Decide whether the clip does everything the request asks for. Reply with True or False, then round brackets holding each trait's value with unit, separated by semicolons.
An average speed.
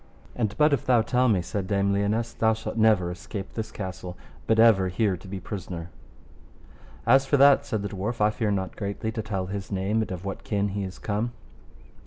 False (210 wpm)